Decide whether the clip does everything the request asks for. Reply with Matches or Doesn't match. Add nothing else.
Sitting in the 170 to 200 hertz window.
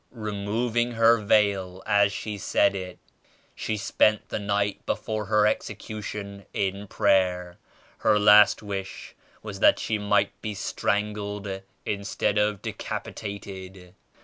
Doesn't match